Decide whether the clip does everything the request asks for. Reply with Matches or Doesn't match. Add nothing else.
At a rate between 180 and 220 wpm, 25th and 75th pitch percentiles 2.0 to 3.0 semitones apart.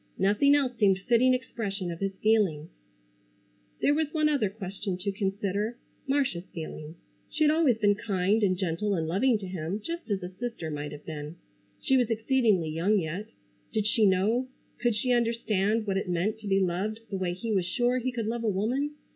Doesn't match